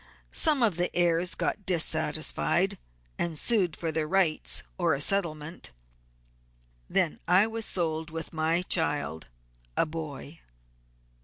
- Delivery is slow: Yes, slow, 125 wpm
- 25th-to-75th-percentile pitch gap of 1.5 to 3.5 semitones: Yes, average, 2.7 semitones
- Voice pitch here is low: No, medium, 165 Hz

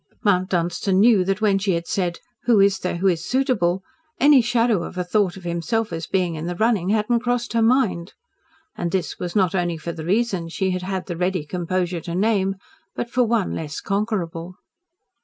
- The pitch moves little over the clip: No, average, 3.9 semitones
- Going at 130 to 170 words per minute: No, fast, 205 wpm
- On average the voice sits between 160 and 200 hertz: Yes, high, 190 Hz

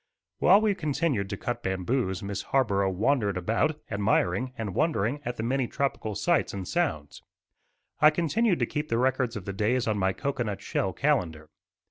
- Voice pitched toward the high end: No, low, 115 Hz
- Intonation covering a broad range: Yes, wide, 6.5 semitones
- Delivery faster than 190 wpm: No, average, 170 wpm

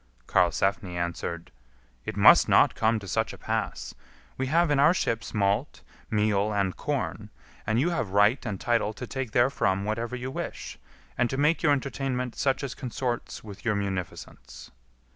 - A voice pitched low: Yes, low, 115 Hz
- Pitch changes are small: No, average, 4.8 semitones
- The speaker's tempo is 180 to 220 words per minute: No, average, 165 wpm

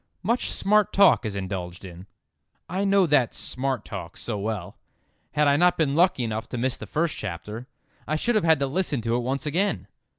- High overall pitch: No, low, 135 Hz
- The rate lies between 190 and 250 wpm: Yes, average, 200 wpm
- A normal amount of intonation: No, wide, 8.1 semitones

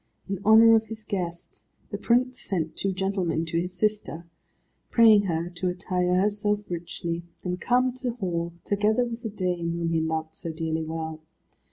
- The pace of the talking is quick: No, average, 170 wpm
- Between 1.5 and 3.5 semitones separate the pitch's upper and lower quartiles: No, average, 4.2 semitones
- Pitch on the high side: No, medium, 180 Hz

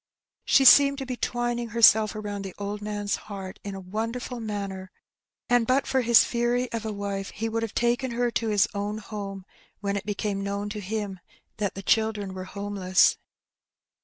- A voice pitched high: Yes, high, 210 Hz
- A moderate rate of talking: Yes, average, 190 wpm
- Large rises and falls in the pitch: No, average, 2.8 semitones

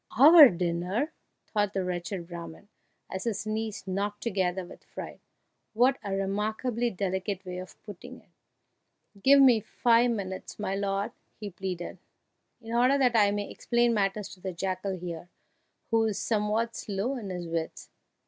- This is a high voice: Yes, high, 200 Hz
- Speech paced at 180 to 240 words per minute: No, average, 155 wpm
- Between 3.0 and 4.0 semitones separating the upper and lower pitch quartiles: Yes, average, 3.5 semitones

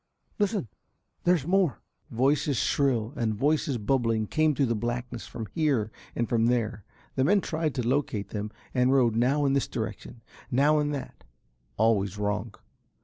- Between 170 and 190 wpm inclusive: No, average, 155 wpm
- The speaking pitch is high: No, low, 125 Hz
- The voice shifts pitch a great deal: No, average, 4.5 semitones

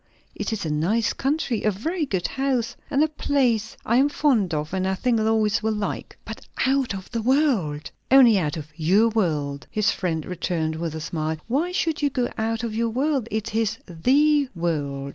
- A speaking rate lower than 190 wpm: No, average, 200 wpm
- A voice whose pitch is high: Yes, high, 220 Hz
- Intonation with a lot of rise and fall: Yes, wide, 7.4 semitones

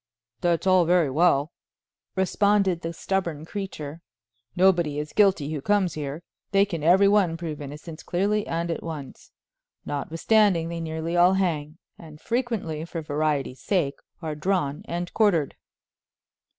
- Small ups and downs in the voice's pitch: No, average, 3.8 semitones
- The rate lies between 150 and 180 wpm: No, average, 140 wpm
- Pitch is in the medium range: Yes, medium, 170 Hz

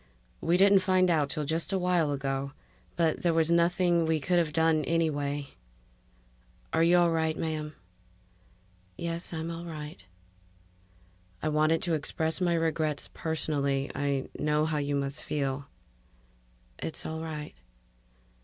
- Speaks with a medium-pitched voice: Yes, medium, 160 Hz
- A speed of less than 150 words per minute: Yes, average, 140 wpm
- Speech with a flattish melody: Yes, narrow, 2.3 semitones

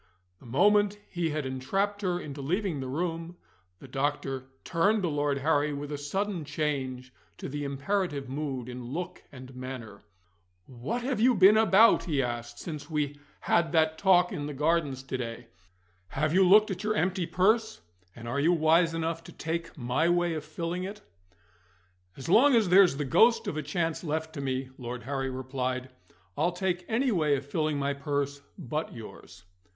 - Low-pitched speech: No, medium, 155 Hz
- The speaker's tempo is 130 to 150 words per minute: No, average, 180 wpm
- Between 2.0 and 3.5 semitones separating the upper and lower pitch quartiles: No, average, 4.9 semitones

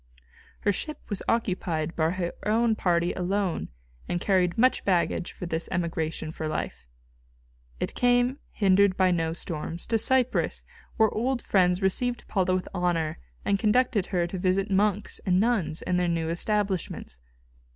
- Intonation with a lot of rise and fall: No, average, 3.6 semitones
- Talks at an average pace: Yes, average, 150 wpm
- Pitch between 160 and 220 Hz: Yes, medium, 185 Hz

